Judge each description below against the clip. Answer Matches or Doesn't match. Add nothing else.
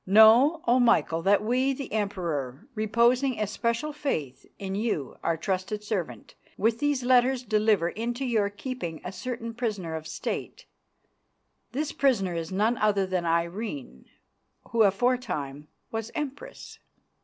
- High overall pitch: Matches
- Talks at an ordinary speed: Doesn't match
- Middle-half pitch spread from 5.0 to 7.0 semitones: Matches